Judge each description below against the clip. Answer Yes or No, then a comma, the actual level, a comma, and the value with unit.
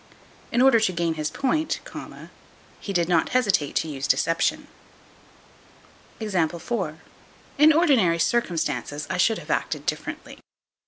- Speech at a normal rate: No, slow, 115 wpm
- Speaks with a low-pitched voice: No, medium, 185 Hz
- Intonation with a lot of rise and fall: Yes, wide, 6.6 semitones